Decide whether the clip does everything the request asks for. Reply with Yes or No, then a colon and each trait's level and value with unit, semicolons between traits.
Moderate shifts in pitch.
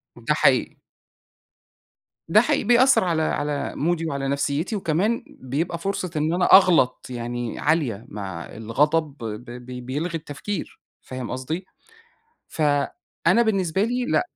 No: wide, 6.1 semitones